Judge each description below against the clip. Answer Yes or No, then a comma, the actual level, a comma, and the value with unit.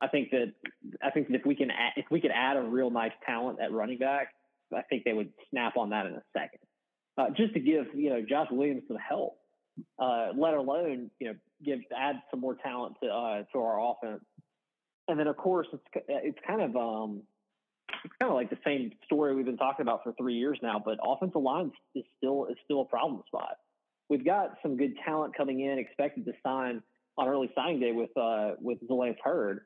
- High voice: No, low, 135 Hz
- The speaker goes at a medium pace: No, fast, 225 wpm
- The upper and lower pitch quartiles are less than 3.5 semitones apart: Yes, average, 3.1 semitones